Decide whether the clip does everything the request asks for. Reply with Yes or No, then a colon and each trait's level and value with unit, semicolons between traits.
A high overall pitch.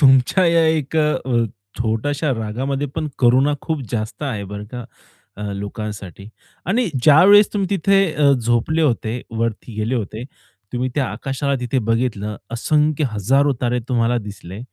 No: low, 125 Hz